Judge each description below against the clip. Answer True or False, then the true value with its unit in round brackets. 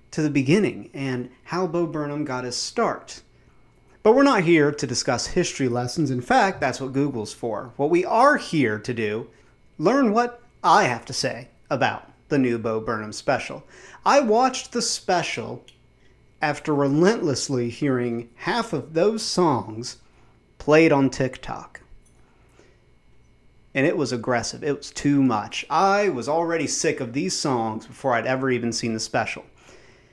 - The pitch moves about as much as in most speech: False (5.7 semitones)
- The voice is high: False (135 Hz)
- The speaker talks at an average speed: True (155 wpm)